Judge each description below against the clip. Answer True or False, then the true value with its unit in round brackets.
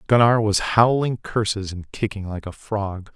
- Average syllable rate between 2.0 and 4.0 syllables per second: False (4.4 syllables/s)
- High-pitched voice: False (105 Hz)